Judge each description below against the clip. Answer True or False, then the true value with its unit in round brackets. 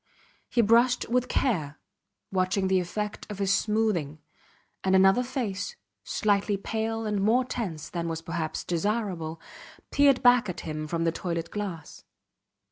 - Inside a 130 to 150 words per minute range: True (140 wpm)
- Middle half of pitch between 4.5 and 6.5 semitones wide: True (4.9 semitones)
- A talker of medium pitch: False (195 Hz)